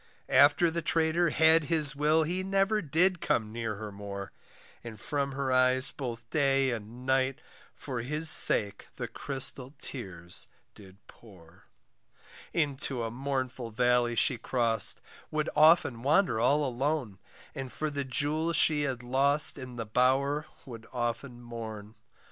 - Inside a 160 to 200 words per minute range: No, average, 140 wpm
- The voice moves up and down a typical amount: Yes, average, 4.3 semitones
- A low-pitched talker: Yes, low, 130 Hz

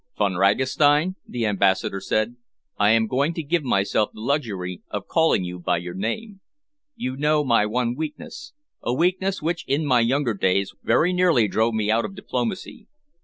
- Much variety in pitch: Yes, wide, 7.2 semitones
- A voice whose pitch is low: Yes, low, 120 Hz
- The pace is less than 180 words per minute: Yes, average, 170 wpm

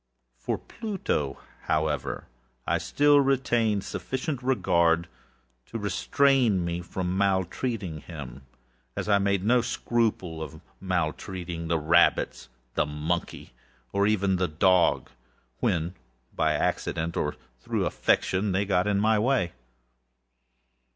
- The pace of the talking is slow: Yes, slow, 115 wpm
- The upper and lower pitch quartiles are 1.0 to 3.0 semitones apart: No, average, 4.8 semitones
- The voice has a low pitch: Yes, very low, 95 Hz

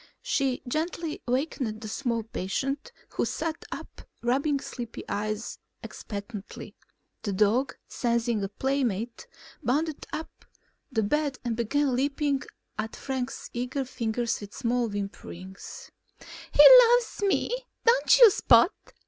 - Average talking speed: No, slow, 125 wpm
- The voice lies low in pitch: No, high, 245 Hz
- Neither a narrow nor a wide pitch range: Yes, average, 4.5 semitones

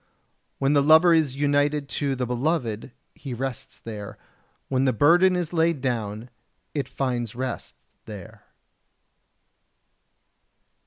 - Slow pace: Yes, slow, 115 wpm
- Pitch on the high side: No, low, 135 Hz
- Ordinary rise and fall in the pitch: Yes, average, 3.6 semitones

